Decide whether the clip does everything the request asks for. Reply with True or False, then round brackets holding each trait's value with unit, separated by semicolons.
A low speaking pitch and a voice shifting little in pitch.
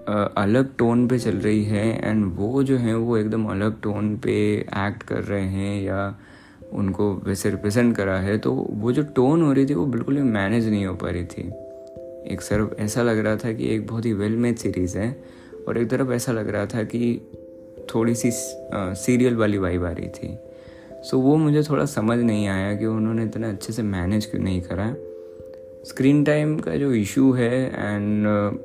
False (110 Hz; 3.7 semitones)